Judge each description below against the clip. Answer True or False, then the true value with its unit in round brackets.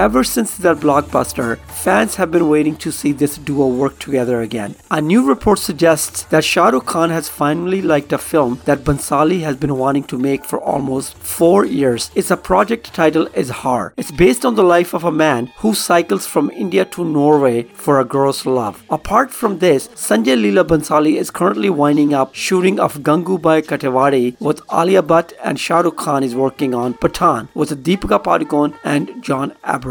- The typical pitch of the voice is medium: True (150 Hz)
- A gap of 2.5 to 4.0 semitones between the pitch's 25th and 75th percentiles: True (3.6 semitones)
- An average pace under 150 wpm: False (185 wpm)